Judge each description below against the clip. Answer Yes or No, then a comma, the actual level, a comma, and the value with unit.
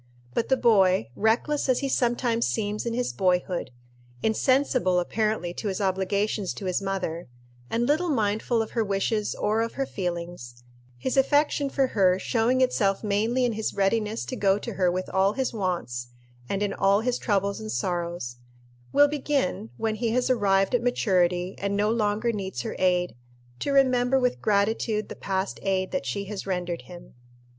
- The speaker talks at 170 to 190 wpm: Yes, average, 175 wpm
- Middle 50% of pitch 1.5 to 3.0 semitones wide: No, average, 4.1 semitones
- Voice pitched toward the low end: No, high, 210 Hz